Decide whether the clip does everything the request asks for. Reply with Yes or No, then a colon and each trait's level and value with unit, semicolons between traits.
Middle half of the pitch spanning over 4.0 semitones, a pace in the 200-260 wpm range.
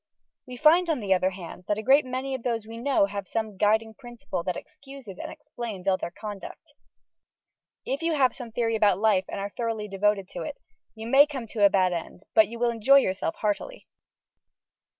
Yes: average, 4.5 semitones; fast, 205 wpm